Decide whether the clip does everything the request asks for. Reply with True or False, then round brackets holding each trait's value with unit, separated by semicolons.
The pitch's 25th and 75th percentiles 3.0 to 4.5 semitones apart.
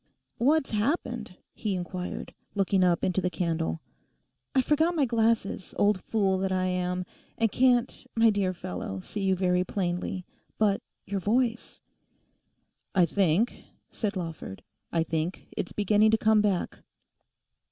True (3.6 semitones)